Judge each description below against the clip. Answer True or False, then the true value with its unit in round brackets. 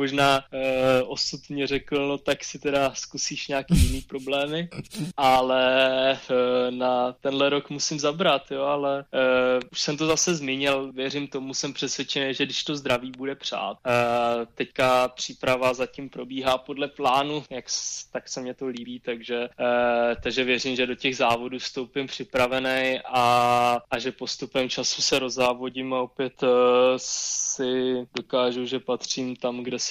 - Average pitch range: False (1.8 semitones)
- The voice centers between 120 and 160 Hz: True (130 Hz)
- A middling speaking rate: True (155 wpm)